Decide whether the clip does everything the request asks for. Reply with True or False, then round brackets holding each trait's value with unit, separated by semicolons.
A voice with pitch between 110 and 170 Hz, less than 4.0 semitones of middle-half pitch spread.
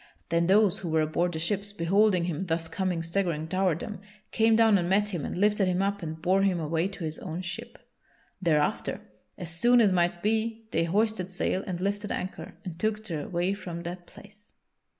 False (185 Hz; 3.4 semitones)